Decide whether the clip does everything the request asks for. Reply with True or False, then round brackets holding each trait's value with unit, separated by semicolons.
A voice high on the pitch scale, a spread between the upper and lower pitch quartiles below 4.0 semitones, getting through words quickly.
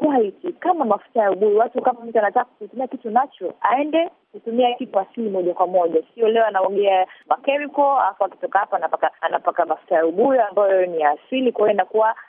False (215 Hz; 5.5 semitones; 180 wpm)